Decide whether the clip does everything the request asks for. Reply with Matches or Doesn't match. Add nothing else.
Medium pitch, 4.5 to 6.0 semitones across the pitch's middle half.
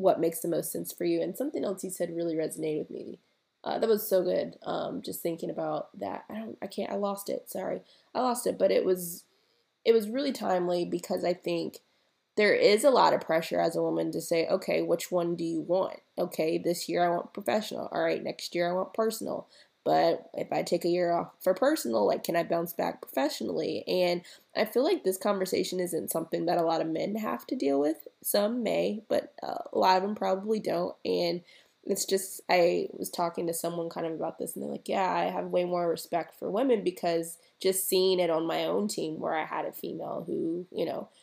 Doesn't match